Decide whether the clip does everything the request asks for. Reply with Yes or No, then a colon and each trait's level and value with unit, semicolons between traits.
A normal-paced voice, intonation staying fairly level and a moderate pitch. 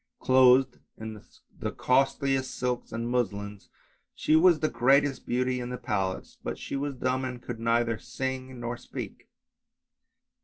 No: average, 145 wpm; narrow, 2.0 semitones; low, 125 Hz